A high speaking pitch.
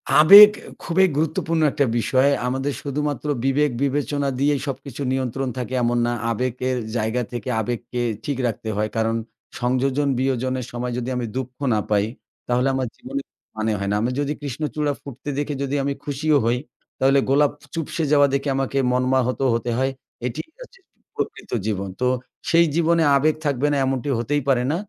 No: low, 135 Hz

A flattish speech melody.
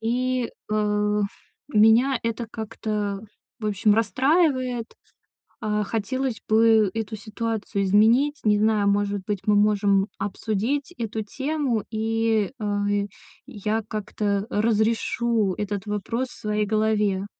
Yes: narrow, 2.1 semitones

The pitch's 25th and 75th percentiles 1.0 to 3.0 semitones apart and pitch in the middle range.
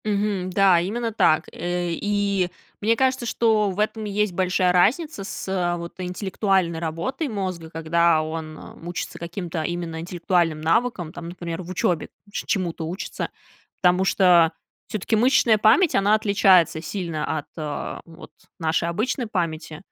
No: average, 3.7 semitones; medium, 180 Hz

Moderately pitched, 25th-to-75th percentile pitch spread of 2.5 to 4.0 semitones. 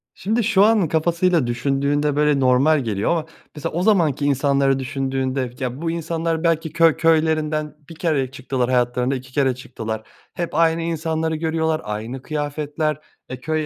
Yes: medium, 150 Hz; average, 3.6 semitones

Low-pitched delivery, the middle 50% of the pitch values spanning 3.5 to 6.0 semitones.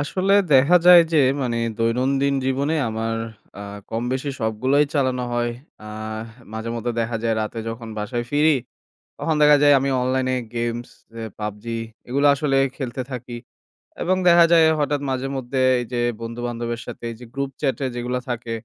No: low, 125 Hz; average, 3.1 semitones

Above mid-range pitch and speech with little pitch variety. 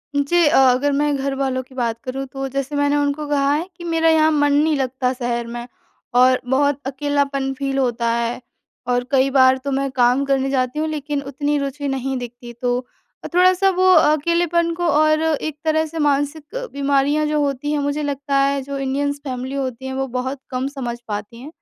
Yes: very high, 275 Hz; narrow, 2.3 semitones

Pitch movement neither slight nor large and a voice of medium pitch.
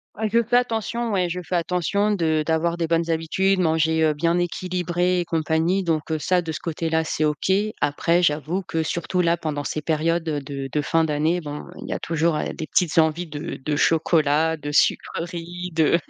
No: narrow, 2.2 semitones; medium, 165 Hz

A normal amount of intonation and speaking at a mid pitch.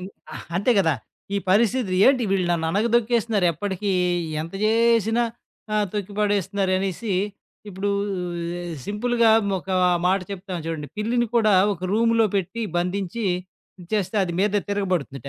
No: average, 3.6 semitones; high, 200 Hz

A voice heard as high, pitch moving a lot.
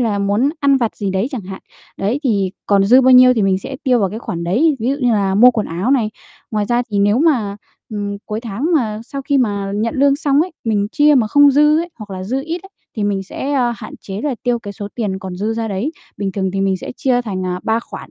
No: high, 220 Hz; average, 4.8 semitones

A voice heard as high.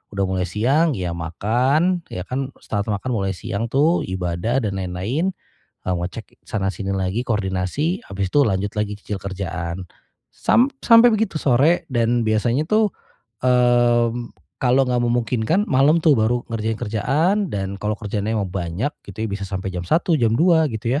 No: low, 115 Hz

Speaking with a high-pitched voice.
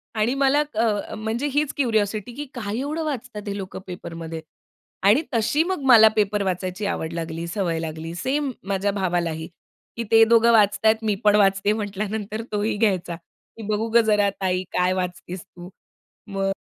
Yes: high, 205 Hz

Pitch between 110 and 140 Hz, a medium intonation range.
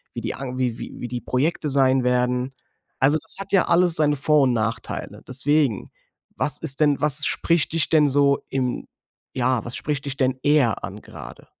Yes: low, 135 Hz; average, 3.0 semitones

